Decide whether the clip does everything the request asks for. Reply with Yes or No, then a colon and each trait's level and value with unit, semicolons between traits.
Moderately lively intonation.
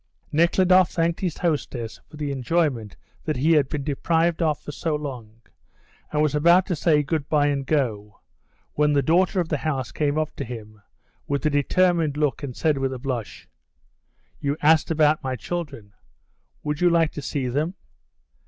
Yes: average, 3.2 semitones